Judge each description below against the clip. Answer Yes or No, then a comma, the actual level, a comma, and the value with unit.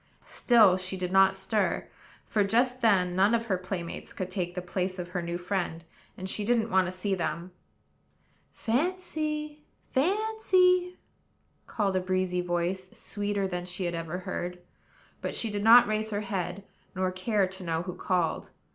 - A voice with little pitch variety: No, average, 3.8 semitones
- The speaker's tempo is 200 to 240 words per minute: No, average, 170 wpm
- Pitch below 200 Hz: Yes, high, 190 Hz